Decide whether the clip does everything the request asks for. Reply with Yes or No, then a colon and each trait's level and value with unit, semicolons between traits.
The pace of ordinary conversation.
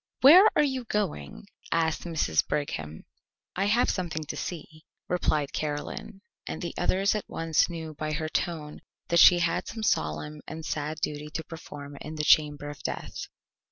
Yes: average, 170 wpm